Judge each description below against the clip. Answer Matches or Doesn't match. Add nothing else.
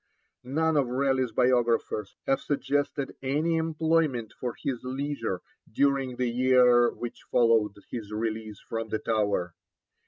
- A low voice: Matches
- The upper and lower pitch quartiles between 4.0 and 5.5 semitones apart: Doesn't match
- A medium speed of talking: Doesn't match